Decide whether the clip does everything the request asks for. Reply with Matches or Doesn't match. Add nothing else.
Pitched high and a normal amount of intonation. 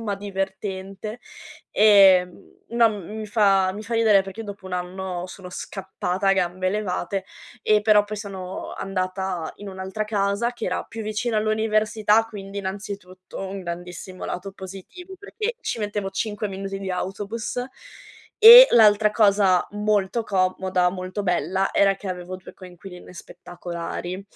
Doesn't match